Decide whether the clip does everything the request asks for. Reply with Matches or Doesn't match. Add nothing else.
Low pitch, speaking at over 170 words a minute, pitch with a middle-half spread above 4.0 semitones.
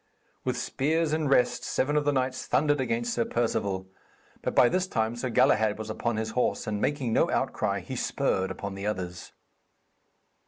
Matches